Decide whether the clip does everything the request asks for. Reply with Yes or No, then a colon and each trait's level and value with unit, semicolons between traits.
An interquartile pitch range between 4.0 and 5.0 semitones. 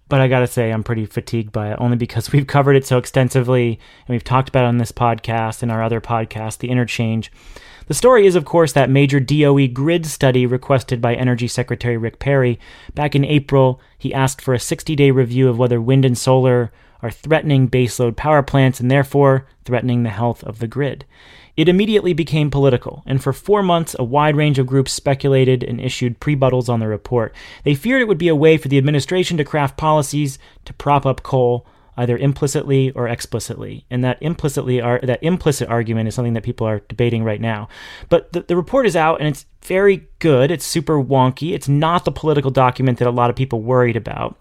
No: average, 3.3 semitones